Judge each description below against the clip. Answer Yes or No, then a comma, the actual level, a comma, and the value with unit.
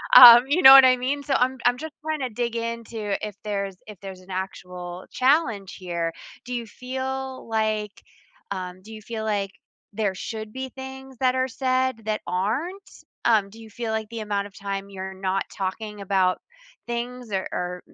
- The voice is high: Yes, high, 220 Hz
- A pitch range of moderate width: Yes, average, 4.5 semitones